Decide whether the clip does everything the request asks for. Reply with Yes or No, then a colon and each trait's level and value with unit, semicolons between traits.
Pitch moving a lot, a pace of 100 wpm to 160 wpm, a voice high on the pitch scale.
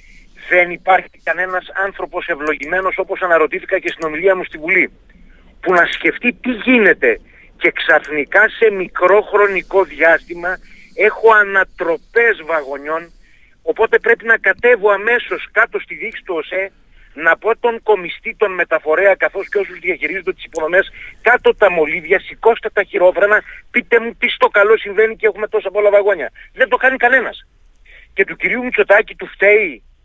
No: average, 4.0 semitones; average, 150 wpm; high, 200 Hz